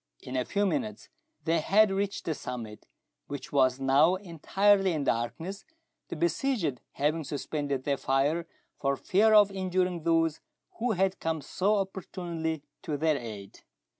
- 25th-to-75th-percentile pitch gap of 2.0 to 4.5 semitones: No, wide, 5.4 semitones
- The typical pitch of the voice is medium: Yes, medium, 165 Hz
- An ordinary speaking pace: Yes, average, 145 wpm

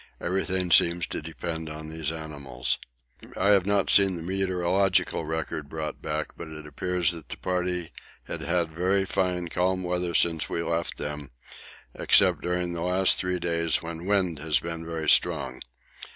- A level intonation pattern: Yes, narrow, 2.2 semitones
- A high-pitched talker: No, very low, 85 Hz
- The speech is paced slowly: No, average, 165 wpm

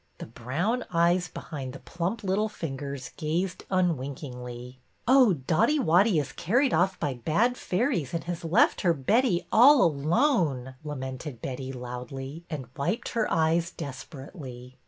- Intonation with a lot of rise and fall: Yes, wide, 6.1 semitones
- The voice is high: No, medium, 160 Hz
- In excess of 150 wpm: No, slow, 135 wpm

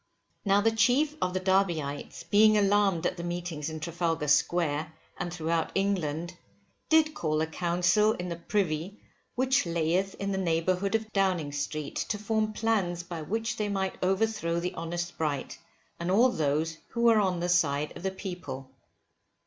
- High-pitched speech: No, medium, 180 Hz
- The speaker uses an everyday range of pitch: Yes, average, 4.0 semitones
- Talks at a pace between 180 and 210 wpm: No, average, 165 wpm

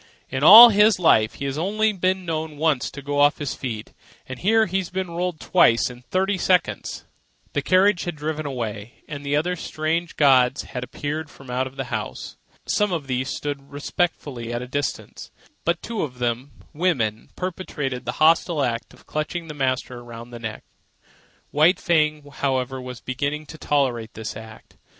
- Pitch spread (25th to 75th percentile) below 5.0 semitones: No, average, 5.3 semitones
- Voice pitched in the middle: Yes, medium, 145 Hz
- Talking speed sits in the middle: Yes, average, 170 wpm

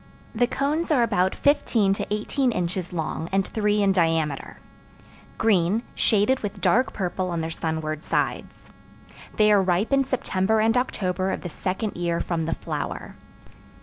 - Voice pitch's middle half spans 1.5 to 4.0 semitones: No, average, 4.4 semitones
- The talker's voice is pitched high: Yes, high, 195 Hz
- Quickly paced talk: No, average, 155 wpm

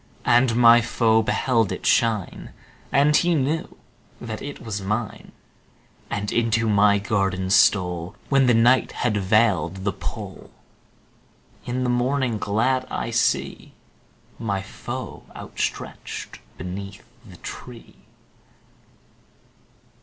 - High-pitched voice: No, low, 115 Hz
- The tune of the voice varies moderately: Yes, average, 3.5 semitones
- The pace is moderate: No, slow, 110 wpm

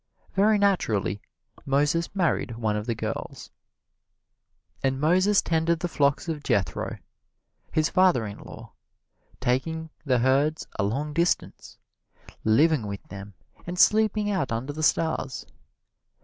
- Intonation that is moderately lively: No, wide, 6.4 semitones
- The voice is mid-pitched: Yes, medium, 150 Hz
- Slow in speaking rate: Yes, slow, 125 wpm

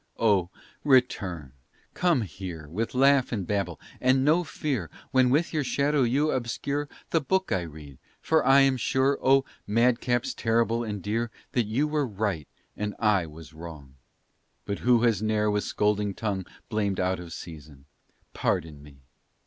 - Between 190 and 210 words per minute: No, average, 155 wpm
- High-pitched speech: No, low, 110 Hz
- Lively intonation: Yes, wide, 6.4 semitones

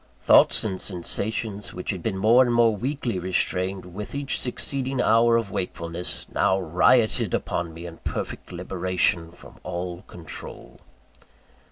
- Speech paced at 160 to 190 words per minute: No, average, 140 wpm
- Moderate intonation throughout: Yes, average, 4.6 semitones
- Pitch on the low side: Yes, very low, 95 Hz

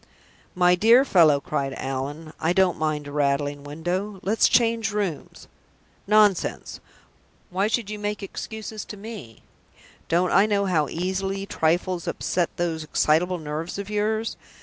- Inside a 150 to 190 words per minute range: No, average, 140 wpm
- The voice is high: No, medium, 180 Hz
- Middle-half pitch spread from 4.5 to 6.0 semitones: Yes, average, 5.0 semitones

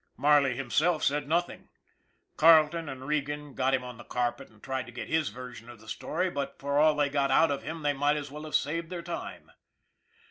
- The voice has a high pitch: No, medium, 145 Hz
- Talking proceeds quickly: Yes, fast, 215 wpm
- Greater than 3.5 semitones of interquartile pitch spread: No, average, 2.9 semitones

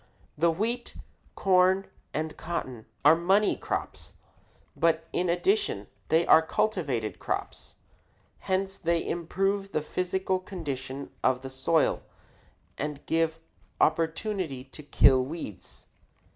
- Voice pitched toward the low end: No, medium, 165 Hz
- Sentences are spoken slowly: Yes, slow, 110 wpm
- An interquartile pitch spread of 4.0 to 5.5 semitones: Yes, average, 4.5 semitones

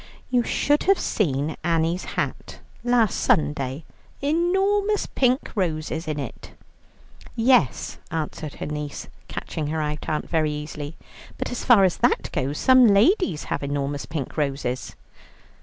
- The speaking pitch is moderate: Yes, medium, 160 Hz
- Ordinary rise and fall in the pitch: No, wide, 8.7 semitones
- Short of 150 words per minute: Yes, slow, 135 wpm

